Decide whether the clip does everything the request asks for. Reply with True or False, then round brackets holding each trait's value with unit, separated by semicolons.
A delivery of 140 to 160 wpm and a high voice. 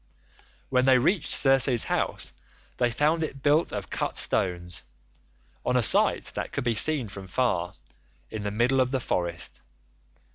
False (155 wpm; 125 Hz)